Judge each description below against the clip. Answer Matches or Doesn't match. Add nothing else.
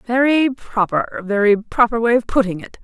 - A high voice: Matches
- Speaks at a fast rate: Doesn't match